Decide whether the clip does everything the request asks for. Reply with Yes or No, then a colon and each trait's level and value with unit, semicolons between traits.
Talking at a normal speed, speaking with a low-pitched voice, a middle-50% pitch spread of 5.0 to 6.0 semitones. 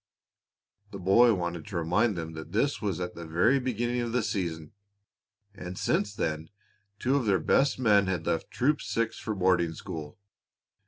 Yes: average, 170 wpm; low, 100 Hz; average, 5.3 semitones